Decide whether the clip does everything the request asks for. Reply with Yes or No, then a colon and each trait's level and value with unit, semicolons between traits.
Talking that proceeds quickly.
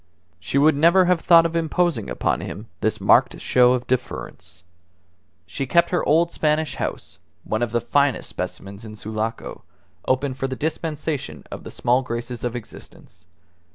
No: average, 160 wpm